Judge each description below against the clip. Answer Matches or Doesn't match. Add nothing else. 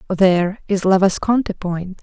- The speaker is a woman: Matches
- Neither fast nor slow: Matches